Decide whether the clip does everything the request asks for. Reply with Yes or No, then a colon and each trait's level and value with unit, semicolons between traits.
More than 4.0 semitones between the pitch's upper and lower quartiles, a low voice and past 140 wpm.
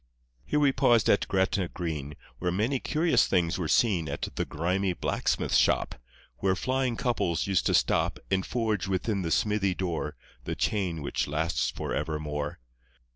Yes: average, 4.6 semitones; very low, 95 Hz; average, 160 wpm